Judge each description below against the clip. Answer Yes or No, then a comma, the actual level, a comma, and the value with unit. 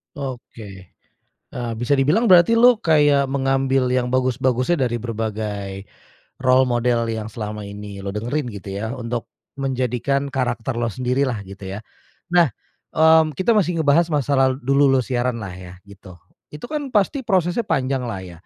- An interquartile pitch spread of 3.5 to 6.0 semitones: Yes, average, 4.4 semitones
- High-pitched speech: No, low, 130 Hz